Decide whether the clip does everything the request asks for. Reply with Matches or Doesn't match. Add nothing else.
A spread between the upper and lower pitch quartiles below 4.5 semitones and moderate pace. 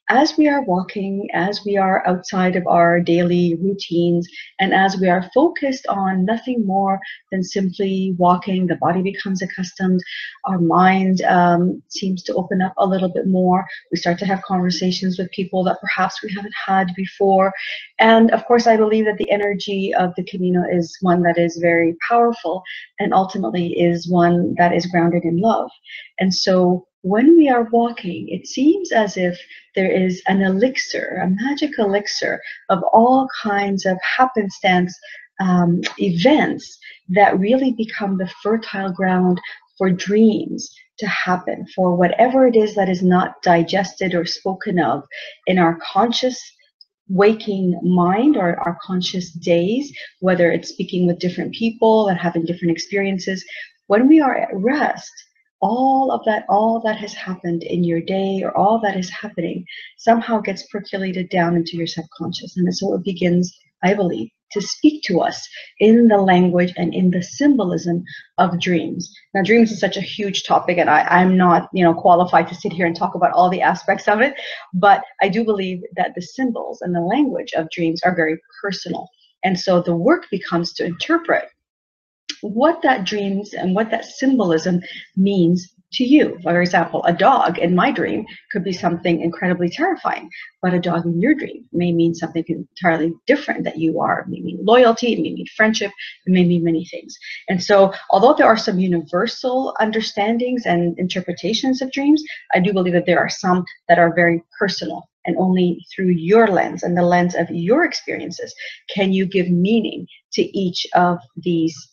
Matches